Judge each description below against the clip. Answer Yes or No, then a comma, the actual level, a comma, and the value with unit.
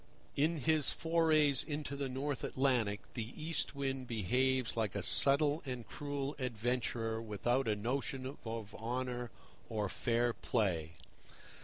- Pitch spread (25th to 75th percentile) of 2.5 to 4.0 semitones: Yes, average, 3.7 semitones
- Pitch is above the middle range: No, low, 125 Hz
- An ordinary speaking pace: No, slow, 130 wpm